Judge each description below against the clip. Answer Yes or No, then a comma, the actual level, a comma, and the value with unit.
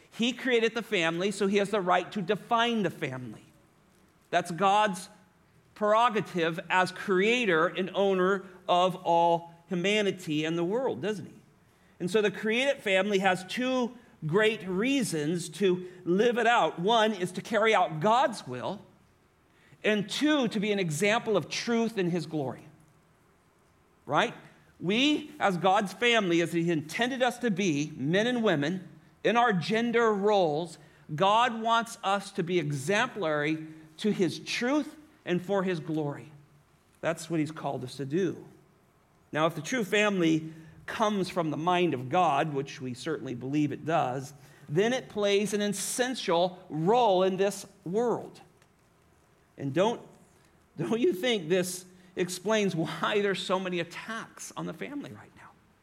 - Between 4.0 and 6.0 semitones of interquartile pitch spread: Yes, average, 4.5 semitones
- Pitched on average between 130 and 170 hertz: No, medium, 185 Hz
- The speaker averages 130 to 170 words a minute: Yes, average, 150 wpm